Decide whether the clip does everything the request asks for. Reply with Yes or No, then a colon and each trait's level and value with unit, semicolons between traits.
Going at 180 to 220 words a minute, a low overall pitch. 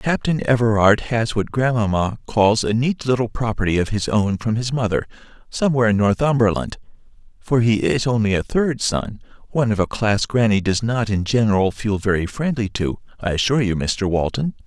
Yes: average, 185 wpm; low, 110 Hz